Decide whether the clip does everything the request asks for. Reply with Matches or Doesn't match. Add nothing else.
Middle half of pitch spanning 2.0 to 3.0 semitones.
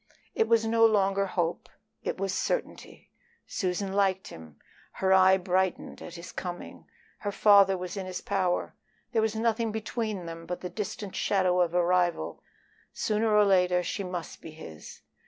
Matches